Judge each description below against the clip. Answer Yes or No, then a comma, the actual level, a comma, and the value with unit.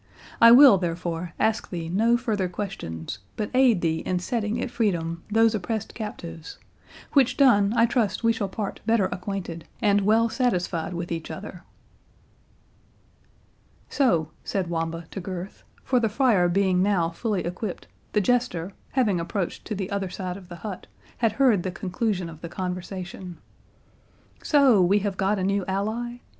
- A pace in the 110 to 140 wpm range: No, average, 155 wpm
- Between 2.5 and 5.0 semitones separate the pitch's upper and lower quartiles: Yes, average, 4.1 semitones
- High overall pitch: Yes, high, 195 Hz